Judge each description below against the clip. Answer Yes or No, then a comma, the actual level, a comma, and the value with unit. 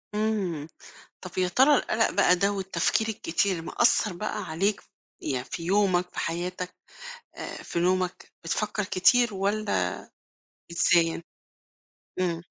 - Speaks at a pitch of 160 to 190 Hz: Yes, medium, 185 Hz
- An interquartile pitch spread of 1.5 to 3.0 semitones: No, average, 3.5 semitones